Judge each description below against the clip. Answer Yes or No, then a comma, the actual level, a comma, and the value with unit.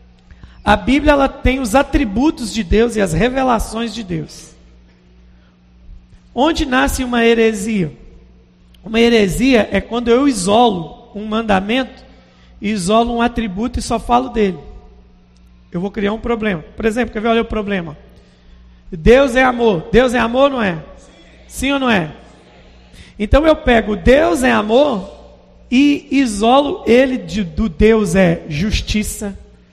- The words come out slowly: No, average, 140 wpm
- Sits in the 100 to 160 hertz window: No, high, 225 Hz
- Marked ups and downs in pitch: Yes, wide, 5.8 semitones